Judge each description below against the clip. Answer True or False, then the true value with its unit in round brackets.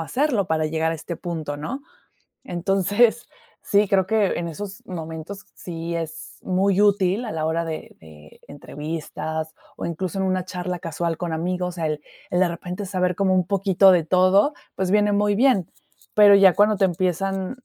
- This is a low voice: False (180 Hz)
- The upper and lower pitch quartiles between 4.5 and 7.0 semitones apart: False (3.4 semitones)